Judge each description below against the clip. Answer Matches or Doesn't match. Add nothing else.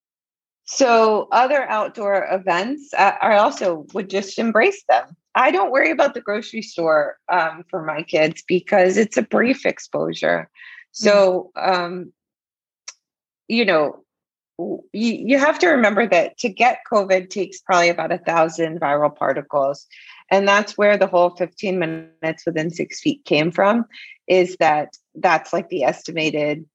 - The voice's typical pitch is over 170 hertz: Matches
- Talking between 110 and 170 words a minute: Matches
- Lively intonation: Matches